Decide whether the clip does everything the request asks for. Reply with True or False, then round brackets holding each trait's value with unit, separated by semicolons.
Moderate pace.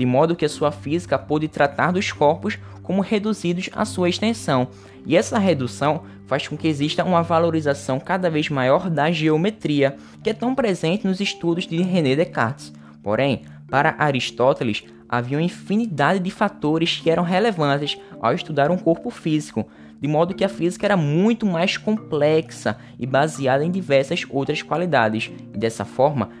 True (165 wpm)